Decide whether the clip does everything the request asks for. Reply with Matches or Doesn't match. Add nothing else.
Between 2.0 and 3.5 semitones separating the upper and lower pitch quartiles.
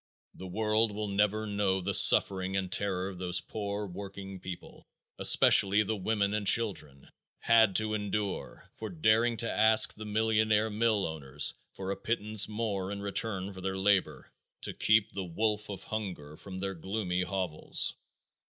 Matches